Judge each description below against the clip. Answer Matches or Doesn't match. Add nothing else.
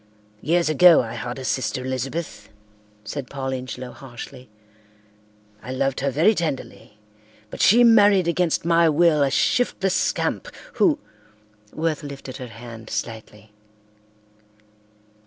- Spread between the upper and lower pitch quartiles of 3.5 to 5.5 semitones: Matches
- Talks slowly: Matches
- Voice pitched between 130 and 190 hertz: Matches